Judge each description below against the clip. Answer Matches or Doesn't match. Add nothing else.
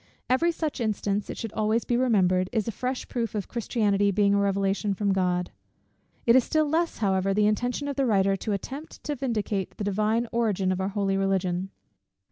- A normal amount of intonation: Matches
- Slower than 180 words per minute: Doesn't match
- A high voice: Matches